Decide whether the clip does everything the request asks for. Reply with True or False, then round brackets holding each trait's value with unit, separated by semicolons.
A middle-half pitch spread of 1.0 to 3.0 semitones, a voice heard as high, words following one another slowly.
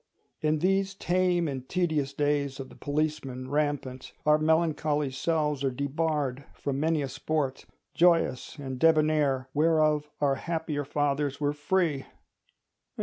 False (2.4 semitones; 150 Hz; 130 wpm)